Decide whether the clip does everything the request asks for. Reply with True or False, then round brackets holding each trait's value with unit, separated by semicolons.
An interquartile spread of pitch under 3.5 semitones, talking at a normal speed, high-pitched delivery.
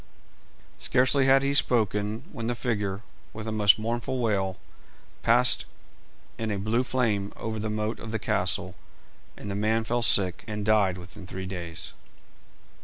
False (2.6 semitones; 155 wpm; 110 Hz)